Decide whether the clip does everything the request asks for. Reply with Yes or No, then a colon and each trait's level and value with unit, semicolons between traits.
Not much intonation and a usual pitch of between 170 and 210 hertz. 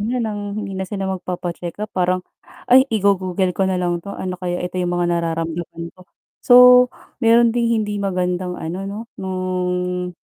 Yes: narrow, 2.2 semitones; medium, 185 Hz